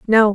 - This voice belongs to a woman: Yes, female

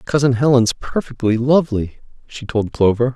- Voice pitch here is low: Yes, low, 125 Hz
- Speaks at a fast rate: No, slow, 135 wpm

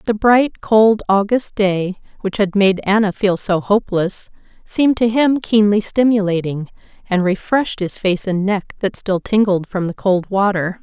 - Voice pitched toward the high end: Yes, high, 200 Hz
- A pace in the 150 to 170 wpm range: Yes, average, 165 wpm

